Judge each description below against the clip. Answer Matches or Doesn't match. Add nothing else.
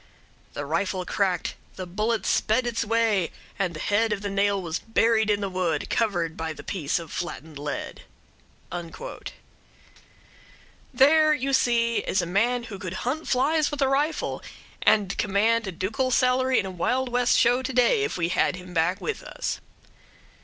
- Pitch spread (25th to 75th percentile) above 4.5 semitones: Matches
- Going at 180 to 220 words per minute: Doesn't match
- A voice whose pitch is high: Matches